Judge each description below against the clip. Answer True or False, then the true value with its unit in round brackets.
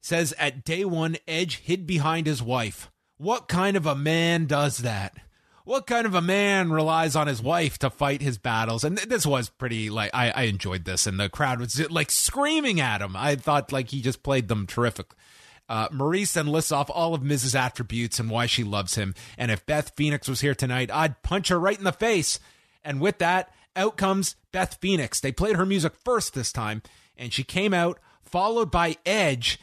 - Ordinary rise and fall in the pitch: False (6.3 semitones)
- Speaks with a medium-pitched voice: True (145 Hz)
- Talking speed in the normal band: False (210 wpm)